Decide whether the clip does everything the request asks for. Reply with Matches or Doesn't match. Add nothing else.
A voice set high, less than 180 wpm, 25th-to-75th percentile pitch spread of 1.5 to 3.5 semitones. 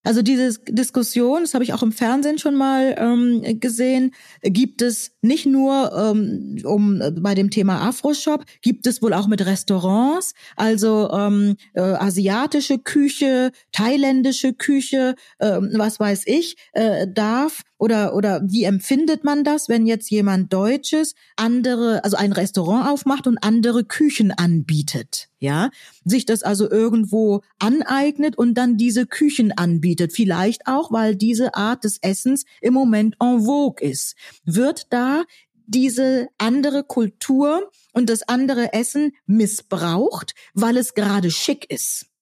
Doesn't match